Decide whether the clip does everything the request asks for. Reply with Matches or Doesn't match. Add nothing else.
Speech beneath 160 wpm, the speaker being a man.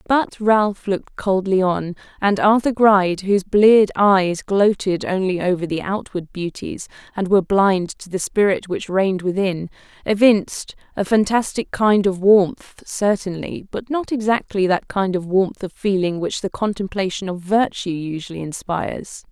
Doesn't match